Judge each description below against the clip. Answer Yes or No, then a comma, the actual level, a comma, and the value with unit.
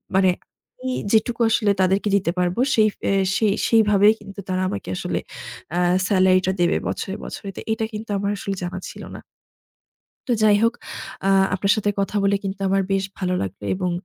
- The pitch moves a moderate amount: No, narrow, 2.2 semitones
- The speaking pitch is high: Yes, high, 195 Hz